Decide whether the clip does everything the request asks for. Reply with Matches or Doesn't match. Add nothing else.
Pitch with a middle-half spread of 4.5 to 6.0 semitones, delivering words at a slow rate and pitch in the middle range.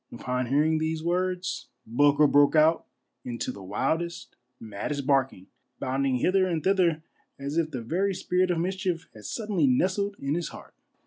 Doesn't match